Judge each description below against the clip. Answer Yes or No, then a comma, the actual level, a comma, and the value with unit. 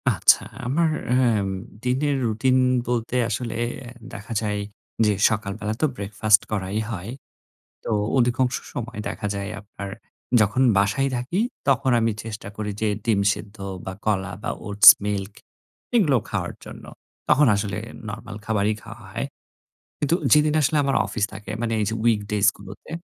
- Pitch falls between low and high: No, low, 110 Hz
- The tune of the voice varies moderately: Yes, average, 3.6 semitones